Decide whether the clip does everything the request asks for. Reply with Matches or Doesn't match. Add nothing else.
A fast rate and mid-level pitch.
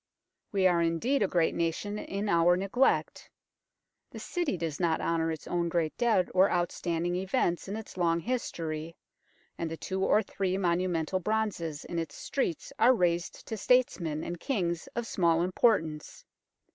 Doesn't match